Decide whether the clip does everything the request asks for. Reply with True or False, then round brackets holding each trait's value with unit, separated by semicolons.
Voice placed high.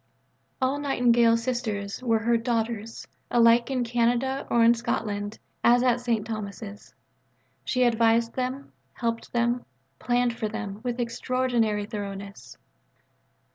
True (235 Hz)